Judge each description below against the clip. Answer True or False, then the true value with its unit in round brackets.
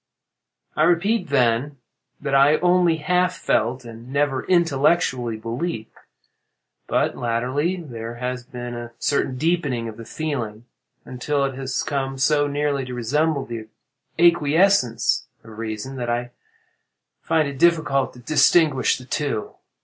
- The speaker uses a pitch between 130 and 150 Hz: True (135 Hz)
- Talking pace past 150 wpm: False (135 wpm)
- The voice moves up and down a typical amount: True (4.5 semitones)